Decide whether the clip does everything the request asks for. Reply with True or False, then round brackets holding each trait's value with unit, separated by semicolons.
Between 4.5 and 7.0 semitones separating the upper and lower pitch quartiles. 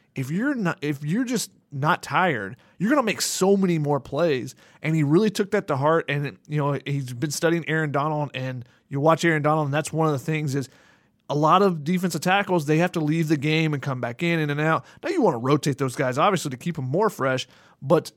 False (3.2 semitones)